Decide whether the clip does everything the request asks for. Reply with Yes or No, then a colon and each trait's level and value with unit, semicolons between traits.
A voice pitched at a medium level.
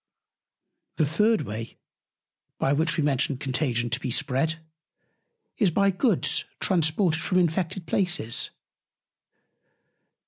Yes: medium, 160 Hz